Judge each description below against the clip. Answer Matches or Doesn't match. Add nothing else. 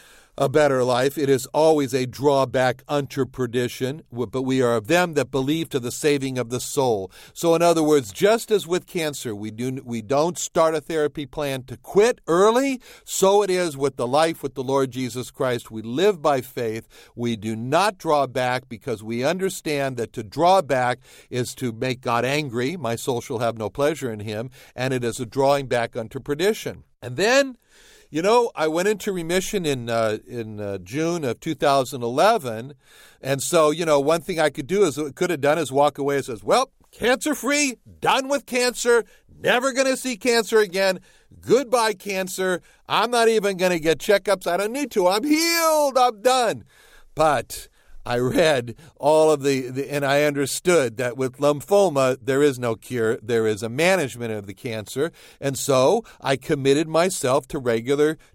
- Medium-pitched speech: Matches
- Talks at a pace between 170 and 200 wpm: Matches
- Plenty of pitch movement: Matches